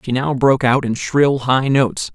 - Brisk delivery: Yes, fast, 225 wpm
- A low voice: Yes, low, 130 Hz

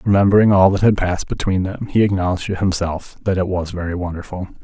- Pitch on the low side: Yes, very low, 95 Hz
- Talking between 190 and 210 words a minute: Yes, fast, 205 wpm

